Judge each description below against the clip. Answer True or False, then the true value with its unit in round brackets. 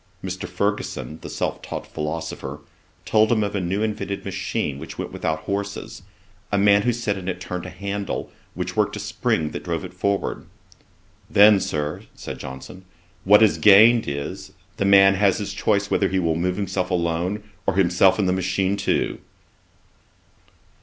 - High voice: False (95 Hz)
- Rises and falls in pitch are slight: True (2.3 semitones)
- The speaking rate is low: False (170 wpm)